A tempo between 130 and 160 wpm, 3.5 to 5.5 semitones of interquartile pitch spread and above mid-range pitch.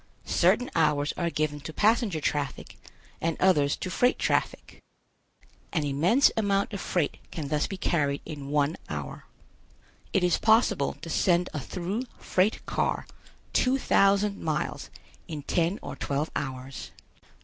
No: average, 140 wpm; average, 5.2 semitones; medium, 165 Hz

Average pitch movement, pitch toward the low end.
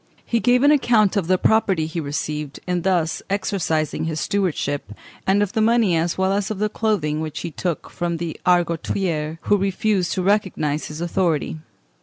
No: average, 4.2 semitones; medium, 180 Hz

